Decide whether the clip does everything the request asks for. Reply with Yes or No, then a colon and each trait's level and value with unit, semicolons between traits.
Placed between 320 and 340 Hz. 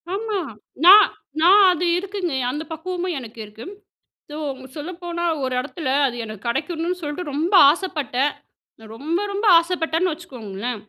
Yes: very high, 325 Hz